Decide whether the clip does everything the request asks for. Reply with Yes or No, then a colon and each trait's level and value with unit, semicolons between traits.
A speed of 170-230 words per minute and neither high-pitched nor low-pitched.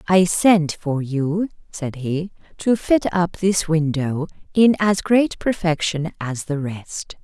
No: average, 150 wpm; medium, 170 Hz